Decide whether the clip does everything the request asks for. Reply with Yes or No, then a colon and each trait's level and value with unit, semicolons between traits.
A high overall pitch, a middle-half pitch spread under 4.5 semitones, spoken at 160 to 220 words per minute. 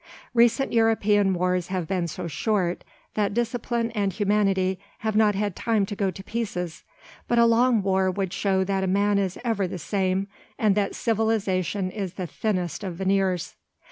Yes: high, 200 Hz; average, 2.8 semitones; average, 170 wpm